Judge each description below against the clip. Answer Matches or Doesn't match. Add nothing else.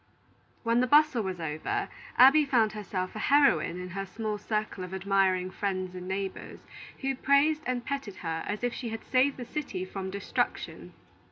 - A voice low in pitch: Doesn't match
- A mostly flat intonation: Doesn't match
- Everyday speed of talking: Matches